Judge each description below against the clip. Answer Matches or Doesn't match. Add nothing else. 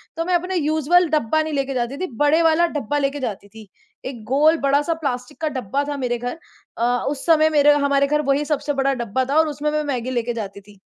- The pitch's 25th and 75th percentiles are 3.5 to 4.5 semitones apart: Matches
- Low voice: Doesn't match